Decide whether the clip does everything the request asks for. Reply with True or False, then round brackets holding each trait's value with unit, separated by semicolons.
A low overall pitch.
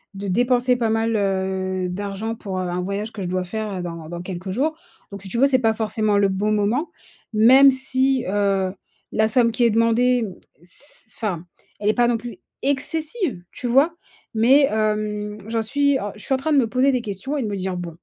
False (220 Hz)